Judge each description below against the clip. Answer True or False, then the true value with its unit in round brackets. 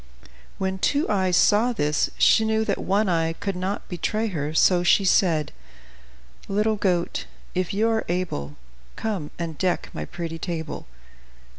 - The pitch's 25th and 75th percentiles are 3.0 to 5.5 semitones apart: True (3.8 semitones)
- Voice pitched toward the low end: False (185 Hz)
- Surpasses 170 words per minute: False (150 wpm)